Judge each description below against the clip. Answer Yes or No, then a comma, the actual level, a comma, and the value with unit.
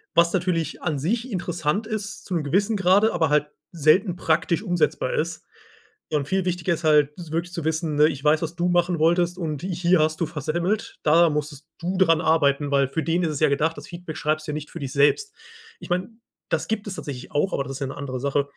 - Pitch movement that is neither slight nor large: Yes, average, 3.2 semitones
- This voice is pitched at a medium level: Yes, medium, 165 Hz